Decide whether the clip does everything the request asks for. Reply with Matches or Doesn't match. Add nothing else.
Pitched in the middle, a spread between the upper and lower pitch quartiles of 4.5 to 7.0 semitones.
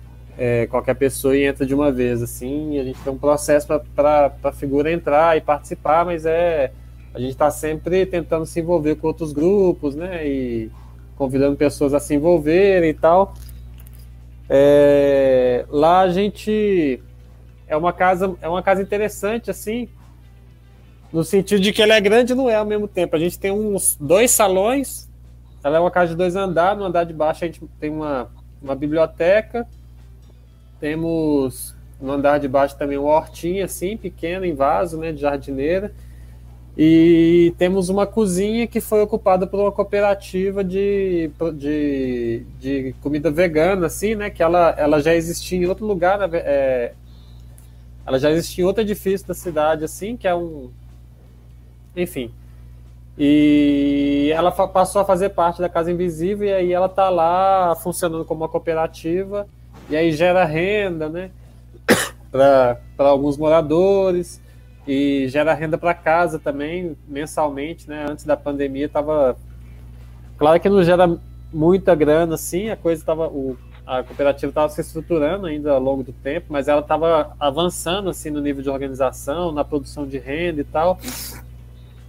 Matches